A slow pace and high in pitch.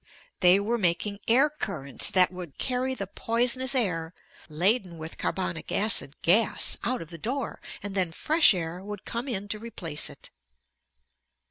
No: average, 155 wpm; high, 200 Hz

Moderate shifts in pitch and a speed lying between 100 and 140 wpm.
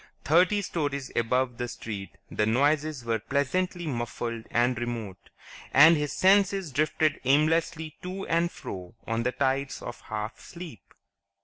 No: wide, 5.7 semitones; slow, 135 wpm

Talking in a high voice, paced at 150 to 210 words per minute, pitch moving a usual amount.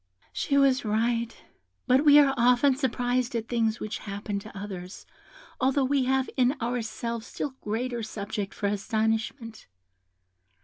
No: high, 235 Hz; slow, 135 wpm; average, 3.1 semitones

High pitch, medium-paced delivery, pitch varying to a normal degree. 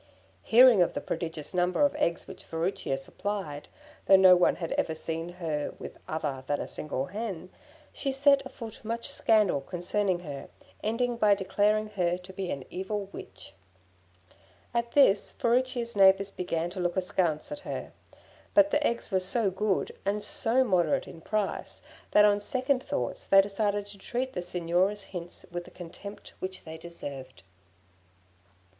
Yes: high, 195 Hz; average, 160 wpm; average, 4.1 semitones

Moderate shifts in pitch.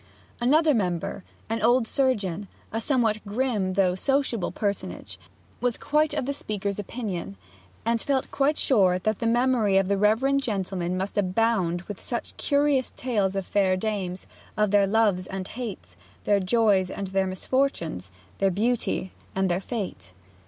Yes: average, 4.3 semitones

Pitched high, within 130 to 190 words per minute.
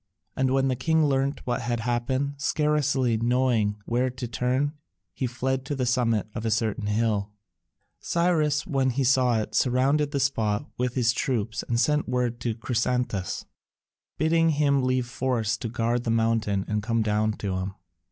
No: low, 125 Hz; average, 170 wpm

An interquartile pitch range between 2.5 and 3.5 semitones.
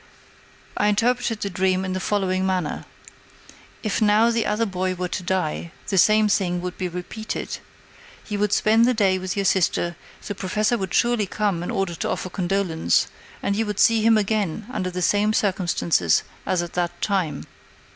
Yes: average, 2.8 semitones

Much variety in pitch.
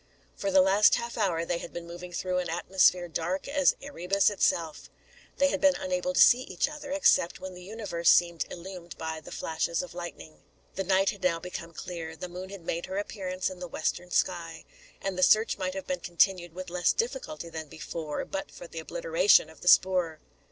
No: average, 3.2 semitones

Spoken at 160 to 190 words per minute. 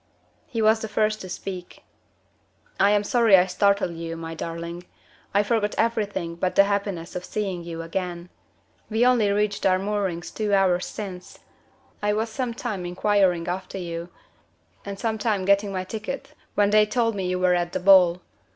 Yes: average, 175 wpm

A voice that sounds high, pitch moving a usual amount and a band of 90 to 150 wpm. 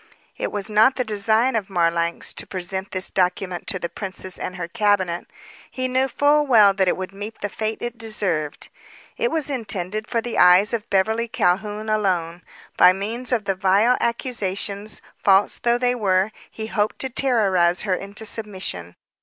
No: high, 205 Hz; average, 3.6 semitones; average, 175 wpm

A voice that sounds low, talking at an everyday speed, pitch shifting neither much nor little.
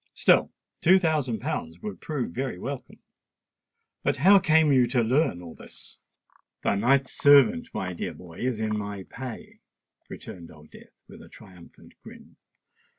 No: low, 125 Hz; average, 150 wpm; wide, 7.3 semitones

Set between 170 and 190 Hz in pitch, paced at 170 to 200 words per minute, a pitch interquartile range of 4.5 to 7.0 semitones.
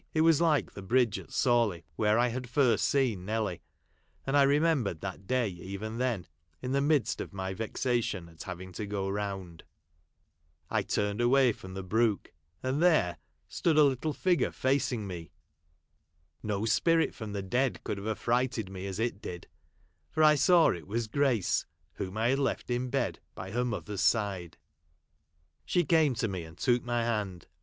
No: low, 115 Hz; average, 180 wpm; average, 5.1 semitones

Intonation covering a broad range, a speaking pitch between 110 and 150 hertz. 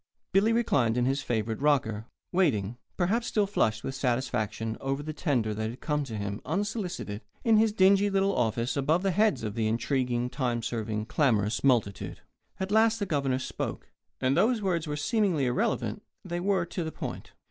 Yes: wide, 8.8 semitones; medium, 140 Hz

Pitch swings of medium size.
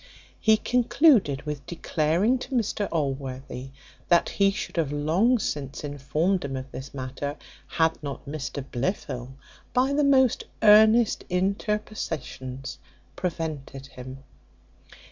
No: wide, 7.5 semitones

